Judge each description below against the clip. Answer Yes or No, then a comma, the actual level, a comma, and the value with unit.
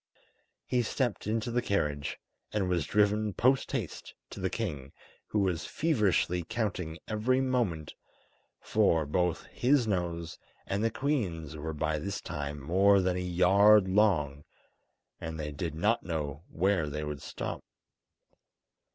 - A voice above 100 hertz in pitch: No, very low, 95 Hz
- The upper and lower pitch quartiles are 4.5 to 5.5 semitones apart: Yes, average, 5.2 semitones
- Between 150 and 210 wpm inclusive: No, average, 140 wpm